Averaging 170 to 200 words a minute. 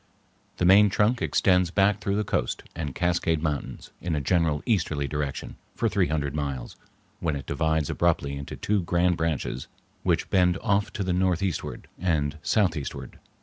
No: average, 160 wpm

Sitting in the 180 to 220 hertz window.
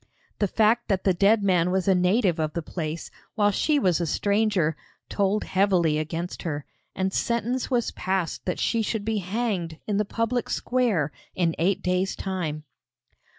Yes: high, 190 Hz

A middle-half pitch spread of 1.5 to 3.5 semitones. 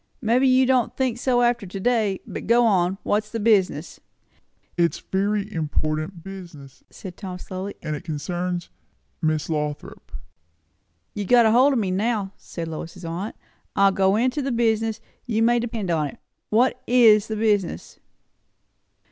No: average, 4.9 semitones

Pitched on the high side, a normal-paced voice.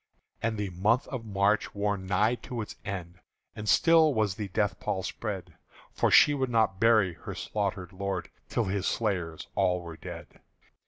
No: low, 100 Hz; average, 170 wpm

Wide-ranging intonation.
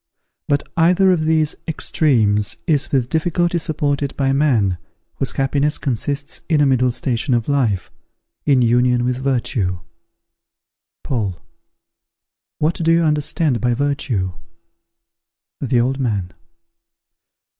No: average, 4.0 semitones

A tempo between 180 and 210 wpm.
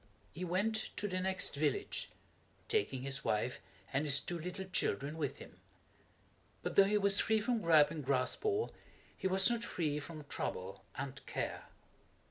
No: average, 160 wpm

